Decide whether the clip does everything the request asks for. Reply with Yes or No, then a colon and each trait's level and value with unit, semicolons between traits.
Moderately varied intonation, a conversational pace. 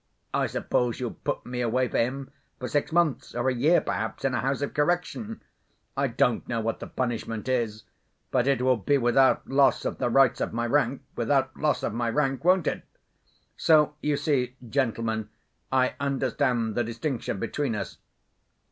Yes: average, 3.0 semitones; average, 175 wpm